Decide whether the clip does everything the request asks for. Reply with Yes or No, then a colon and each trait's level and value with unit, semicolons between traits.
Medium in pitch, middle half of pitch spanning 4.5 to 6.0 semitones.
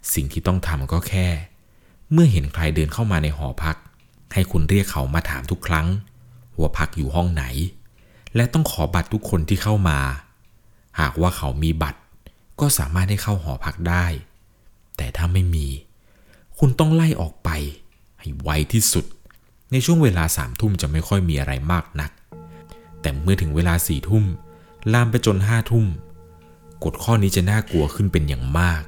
No: very low, 85 Hz; average, 5.1 semitones